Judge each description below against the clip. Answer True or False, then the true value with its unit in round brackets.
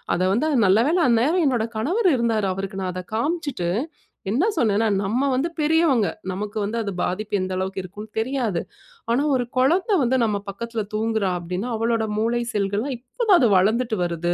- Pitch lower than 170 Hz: False (225 Hz)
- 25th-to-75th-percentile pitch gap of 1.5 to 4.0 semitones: False (4.7 semitones)